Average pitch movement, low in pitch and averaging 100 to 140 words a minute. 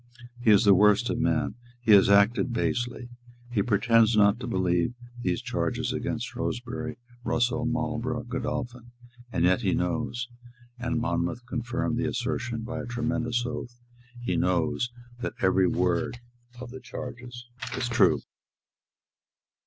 Yes: average, 3.1 semitones; low, 120 Hz; slow, 135 wpm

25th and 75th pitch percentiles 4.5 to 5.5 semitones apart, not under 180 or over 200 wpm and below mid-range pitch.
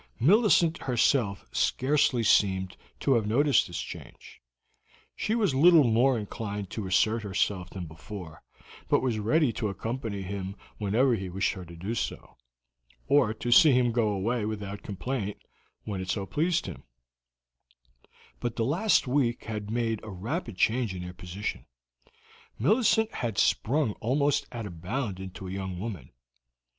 No: average, 5.1 semitones; average, 150 wpm; low, 110 Hz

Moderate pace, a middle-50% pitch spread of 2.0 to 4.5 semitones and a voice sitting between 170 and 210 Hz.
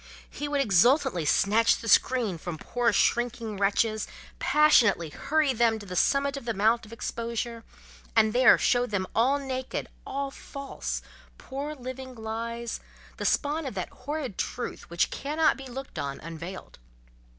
No: average, 145 wpm; average, 4.0 semitones; high, 235 Hz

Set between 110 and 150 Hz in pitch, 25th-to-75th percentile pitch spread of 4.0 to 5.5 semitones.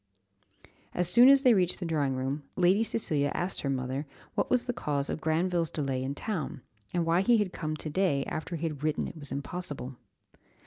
No: medium, 160 Hz; average, 4.5 semitones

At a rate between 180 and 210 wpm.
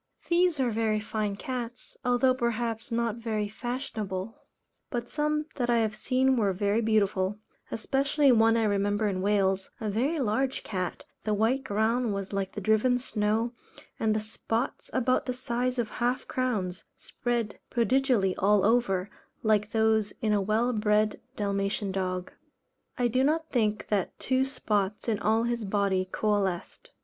No: average, 155 wpm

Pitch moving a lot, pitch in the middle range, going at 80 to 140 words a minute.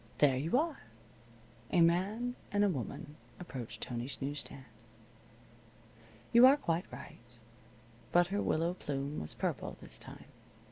Yes: wide, 6.8 semitones; medium, 165 Hz; slow, 135 wpm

